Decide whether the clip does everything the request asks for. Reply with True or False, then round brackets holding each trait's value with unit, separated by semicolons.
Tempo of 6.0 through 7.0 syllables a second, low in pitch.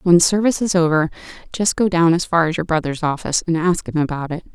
False (6.4 syllables/s; 165 Hz)